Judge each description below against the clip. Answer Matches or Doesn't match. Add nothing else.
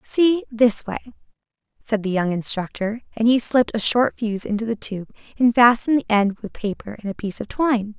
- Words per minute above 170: Matches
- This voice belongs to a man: Doesn't match